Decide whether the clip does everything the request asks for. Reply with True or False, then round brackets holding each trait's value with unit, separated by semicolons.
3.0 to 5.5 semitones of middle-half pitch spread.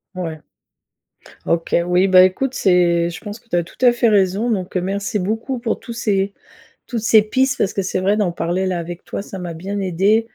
True (3.5 semitones)